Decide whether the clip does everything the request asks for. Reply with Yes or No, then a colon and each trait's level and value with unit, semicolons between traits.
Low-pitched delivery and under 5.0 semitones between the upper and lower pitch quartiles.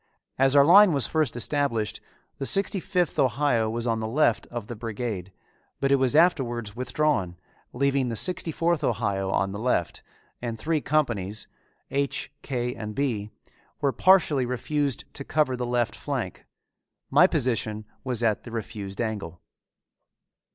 Yes: low, 125 Hz; average, 4.6 semitones